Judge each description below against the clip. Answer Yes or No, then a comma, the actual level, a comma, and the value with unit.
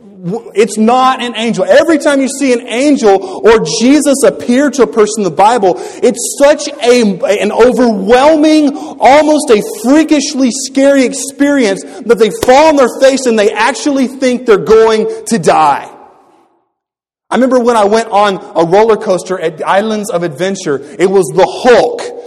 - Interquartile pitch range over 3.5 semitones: Yes, average, 5.2 semitones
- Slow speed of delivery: No, average, 165 wpm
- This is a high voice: Yes, high, 245 Hz